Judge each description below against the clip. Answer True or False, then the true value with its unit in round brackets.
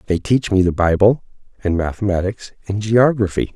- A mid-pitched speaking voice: False (100 Hz)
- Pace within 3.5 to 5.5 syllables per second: True (5.2 syllables/s)